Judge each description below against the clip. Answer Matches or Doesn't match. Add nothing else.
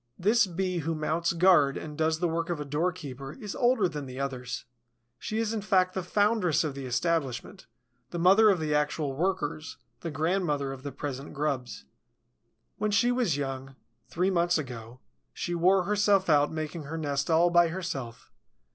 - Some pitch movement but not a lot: Matches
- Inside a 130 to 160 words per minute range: Doesn't match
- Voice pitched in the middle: Matches